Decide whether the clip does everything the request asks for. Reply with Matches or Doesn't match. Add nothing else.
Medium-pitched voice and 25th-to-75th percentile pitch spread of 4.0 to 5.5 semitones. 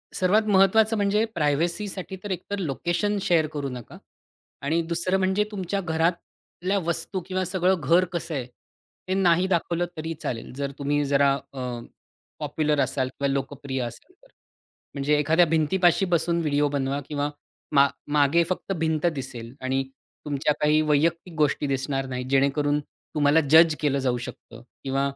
Matches